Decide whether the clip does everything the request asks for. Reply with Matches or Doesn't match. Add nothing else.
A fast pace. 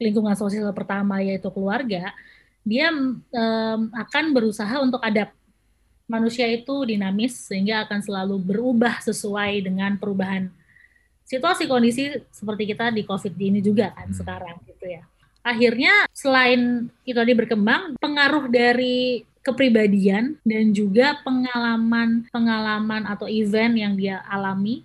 Doesn't match